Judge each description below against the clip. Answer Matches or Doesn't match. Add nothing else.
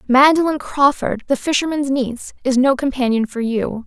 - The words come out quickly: Doesn't match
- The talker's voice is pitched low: Doesn't match